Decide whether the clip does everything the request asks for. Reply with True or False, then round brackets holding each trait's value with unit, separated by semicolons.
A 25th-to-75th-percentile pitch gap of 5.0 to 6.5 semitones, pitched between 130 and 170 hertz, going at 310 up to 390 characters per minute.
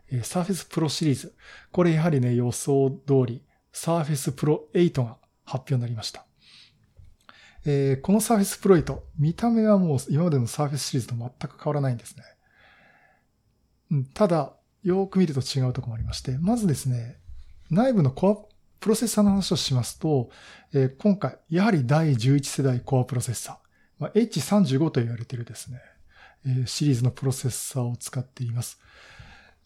True (5.5 semitones; 140 Hz; 355 characters per minute)